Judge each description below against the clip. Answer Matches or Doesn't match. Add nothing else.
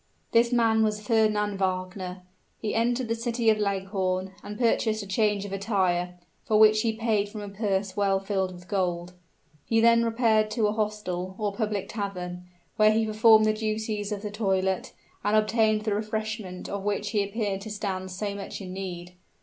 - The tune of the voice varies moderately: Doesn't match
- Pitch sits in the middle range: Doesn't match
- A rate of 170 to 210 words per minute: Matches